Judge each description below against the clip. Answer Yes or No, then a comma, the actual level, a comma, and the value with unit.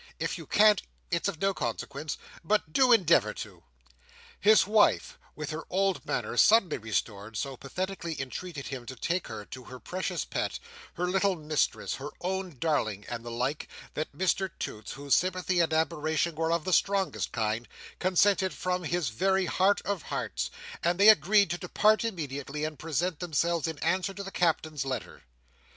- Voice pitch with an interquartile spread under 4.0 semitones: No, average, 5.0 semitones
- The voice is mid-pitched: Yes, medium, 170 Hz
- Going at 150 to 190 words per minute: Yes, average, 170 wpm